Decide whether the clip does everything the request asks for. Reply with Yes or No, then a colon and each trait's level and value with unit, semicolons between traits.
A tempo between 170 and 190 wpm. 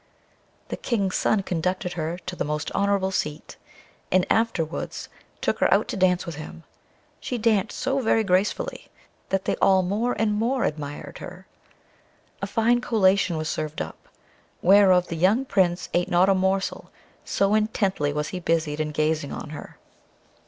No: average, 160 wpm